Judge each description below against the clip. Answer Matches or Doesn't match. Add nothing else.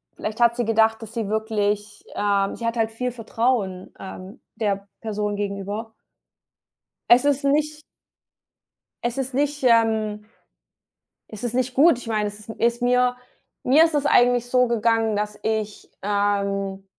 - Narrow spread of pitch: Doesn't match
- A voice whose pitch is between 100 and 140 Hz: Doesn't match